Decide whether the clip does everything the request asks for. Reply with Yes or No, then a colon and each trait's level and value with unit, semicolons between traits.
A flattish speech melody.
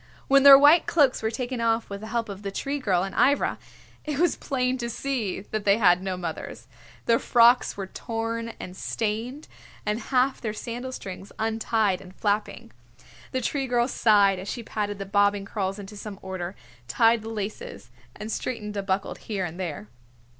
No: average, 3.6 semitones